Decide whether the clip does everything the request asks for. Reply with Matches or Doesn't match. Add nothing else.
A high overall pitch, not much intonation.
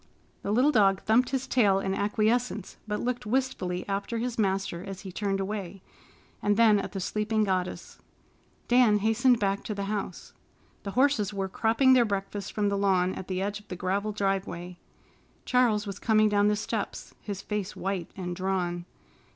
Matches